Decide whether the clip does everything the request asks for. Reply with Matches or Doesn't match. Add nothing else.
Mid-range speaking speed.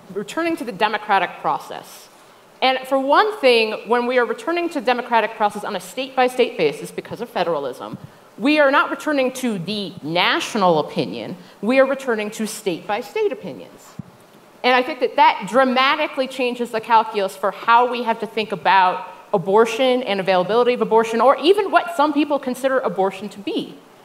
Matches